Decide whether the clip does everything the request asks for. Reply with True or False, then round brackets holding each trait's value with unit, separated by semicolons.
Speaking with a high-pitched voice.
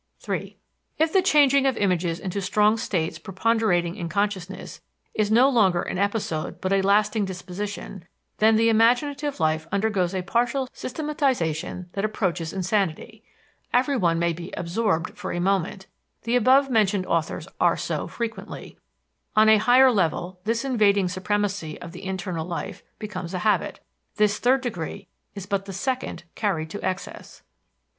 True (200 Hz)